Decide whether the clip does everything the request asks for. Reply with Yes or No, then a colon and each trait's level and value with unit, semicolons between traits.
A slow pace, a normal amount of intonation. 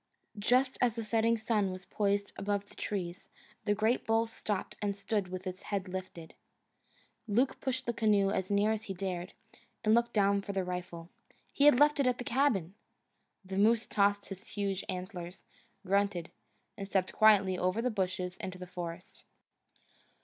No: average, 170 wpm; average, 3.1 semitones